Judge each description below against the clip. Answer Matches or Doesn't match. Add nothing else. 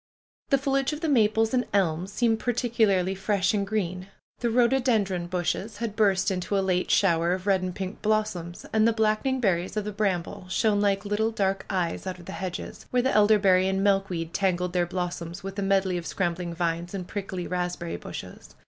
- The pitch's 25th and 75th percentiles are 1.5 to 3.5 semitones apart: Matches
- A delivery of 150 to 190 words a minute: Doesn't match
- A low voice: Doesn't match